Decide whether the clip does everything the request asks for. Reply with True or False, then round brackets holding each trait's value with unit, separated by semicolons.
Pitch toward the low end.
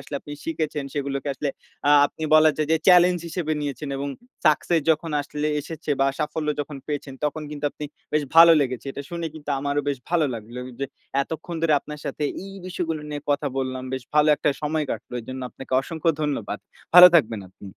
False (150 Hz)